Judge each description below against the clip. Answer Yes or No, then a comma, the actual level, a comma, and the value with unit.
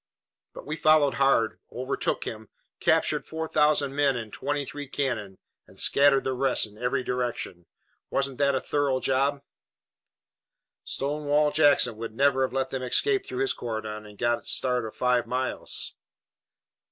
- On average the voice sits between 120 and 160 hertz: Yes, low, 135 Hz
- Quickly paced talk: No, average, 155 wpm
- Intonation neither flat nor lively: Yes, average, 3.0 semitones